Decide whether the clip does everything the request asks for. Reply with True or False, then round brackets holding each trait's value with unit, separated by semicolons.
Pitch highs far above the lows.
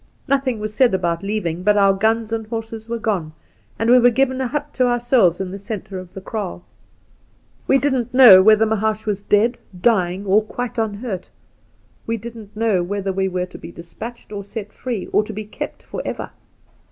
False (3.3 semitones)